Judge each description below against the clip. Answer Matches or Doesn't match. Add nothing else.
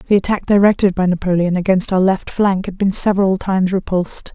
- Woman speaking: Matches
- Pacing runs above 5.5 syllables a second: Matches